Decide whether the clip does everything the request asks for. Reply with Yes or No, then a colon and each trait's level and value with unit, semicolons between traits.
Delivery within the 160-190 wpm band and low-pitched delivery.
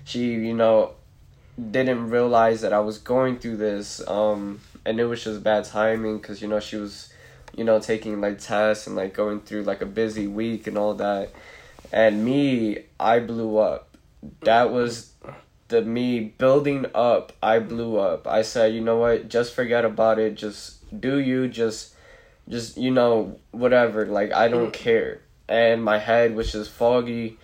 Yes: average, 175 wpm; low, 110 Hz